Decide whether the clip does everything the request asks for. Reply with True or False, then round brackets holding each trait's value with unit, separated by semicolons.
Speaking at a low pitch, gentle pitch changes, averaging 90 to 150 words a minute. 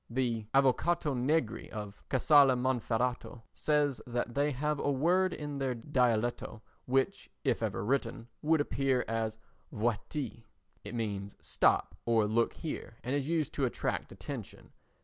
False (125 Hz; 3.8 semitones; 140 wpm)